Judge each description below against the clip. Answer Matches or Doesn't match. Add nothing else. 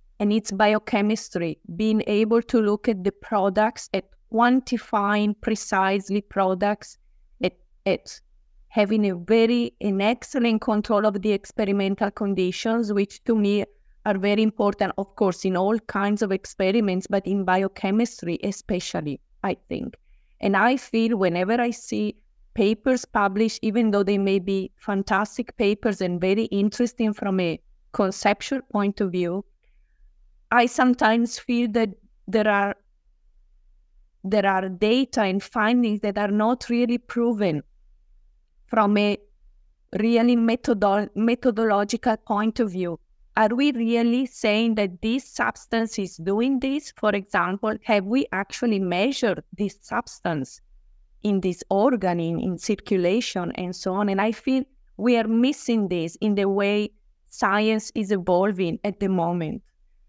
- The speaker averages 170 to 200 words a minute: Doesn't match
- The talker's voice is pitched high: Matches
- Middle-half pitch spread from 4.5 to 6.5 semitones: Doesn't match